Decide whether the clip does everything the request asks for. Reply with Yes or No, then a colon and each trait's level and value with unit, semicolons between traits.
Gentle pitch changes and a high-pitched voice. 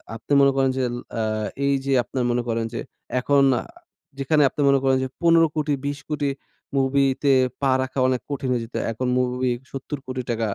No: narrow, 1.9 semitones; low, 135 Hz